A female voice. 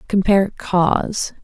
Yes: female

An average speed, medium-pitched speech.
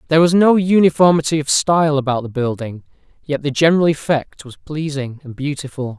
Yes: average, 170 wpm; medium, 150 Hz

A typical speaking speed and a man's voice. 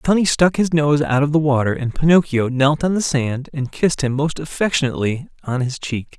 No: fast, 225 wpm; male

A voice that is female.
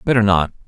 No: male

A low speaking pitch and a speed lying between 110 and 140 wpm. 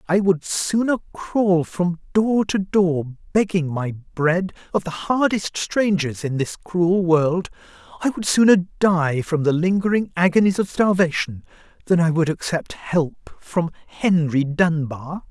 No: medium, 175 Hz; slow, 135 wpm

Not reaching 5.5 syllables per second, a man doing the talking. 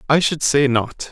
Yes: 4.3 syllables/s; male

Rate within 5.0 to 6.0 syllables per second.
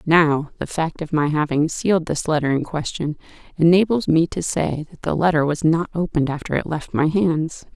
Yes: 5.3 syllables/s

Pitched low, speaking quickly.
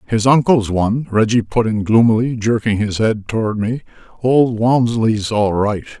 No: low, 110 Hz; average, 160 wpm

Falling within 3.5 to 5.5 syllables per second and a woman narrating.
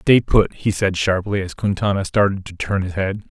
No: 4.9 syllables/s; male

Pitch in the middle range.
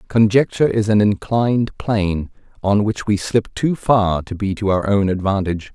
No: low, 105 Hz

